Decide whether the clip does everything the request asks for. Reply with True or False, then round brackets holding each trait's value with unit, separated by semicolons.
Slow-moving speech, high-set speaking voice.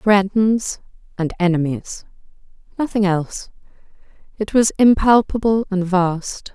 True (80 wpm; 200 Hz)